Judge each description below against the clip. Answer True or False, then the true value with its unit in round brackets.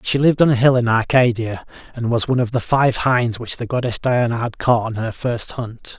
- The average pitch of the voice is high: False (120 Hz)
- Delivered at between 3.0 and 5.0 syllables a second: False (5.4 syllables/s)